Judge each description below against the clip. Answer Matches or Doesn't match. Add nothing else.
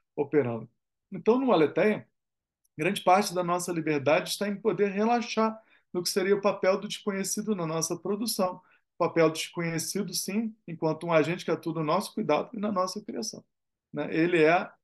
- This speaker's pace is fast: Doesn't match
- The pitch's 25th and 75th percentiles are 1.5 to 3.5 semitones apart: Doesn't match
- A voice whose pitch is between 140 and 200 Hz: Matches